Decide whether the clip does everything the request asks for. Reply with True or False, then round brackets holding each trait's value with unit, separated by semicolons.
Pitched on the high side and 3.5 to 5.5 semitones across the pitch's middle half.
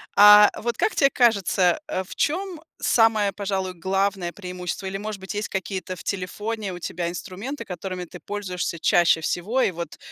False (195 Hz; 2.7 semitones)